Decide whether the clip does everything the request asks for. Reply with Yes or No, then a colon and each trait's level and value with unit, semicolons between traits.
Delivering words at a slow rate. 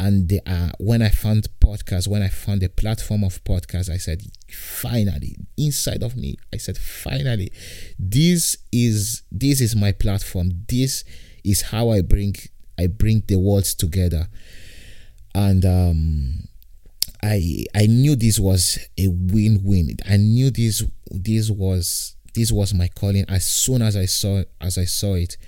No: average, 155 wpm